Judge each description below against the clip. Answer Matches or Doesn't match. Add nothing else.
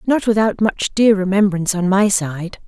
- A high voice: Matches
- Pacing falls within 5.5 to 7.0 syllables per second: Doesn't match